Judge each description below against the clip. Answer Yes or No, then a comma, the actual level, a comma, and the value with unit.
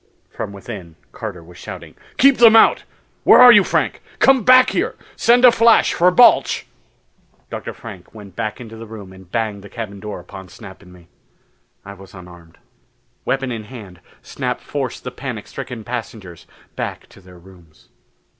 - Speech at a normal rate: Yes, average, 170 wpm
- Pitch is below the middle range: Yes, low, 105 Hz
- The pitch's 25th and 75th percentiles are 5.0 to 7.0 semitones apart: Yes, average, 5.3 semitones